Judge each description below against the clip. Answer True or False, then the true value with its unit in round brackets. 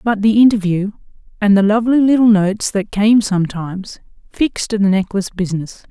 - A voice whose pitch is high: True (205 Hz)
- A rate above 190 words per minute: False (150 wpm)